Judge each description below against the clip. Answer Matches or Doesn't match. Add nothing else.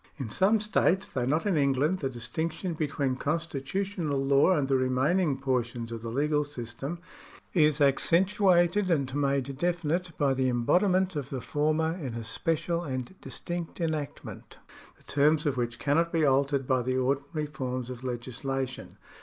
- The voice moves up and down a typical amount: Matches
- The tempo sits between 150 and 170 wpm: Matches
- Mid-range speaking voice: Matches